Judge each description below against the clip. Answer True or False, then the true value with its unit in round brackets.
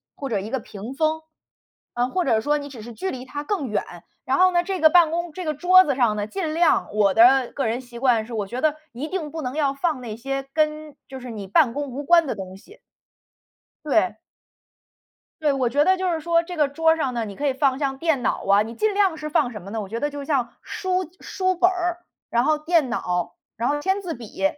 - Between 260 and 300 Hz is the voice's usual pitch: True (285 Hz)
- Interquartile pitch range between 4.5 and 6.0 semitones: True (5.4 semitones)